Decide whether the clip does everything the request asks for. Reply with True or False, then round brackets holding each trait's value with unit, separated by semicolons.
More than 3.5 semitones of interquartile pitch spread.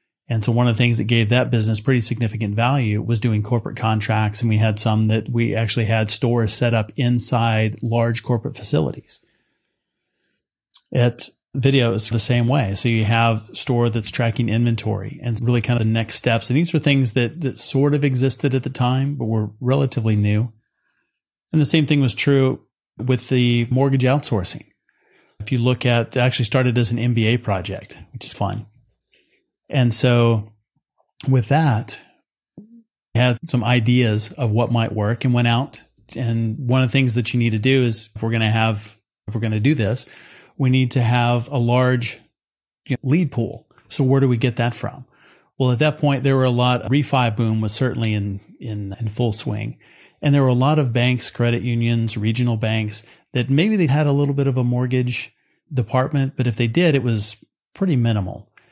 False (2.6 semitones)